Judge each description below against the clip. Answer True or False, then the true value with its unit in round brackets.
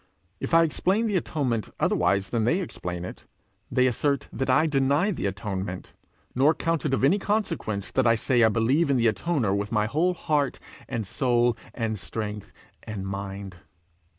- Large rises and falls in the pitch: True (6.6 semitones)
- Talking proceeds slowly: False (175 wpm)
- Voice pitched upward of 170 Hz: False (120 Hz)